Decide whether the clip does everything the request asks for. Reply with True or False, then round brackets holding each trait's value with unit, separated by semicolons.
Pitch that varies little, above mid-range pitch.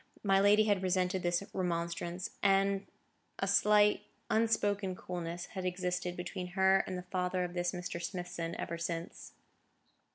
False (1.7 semitones; 180 Hz)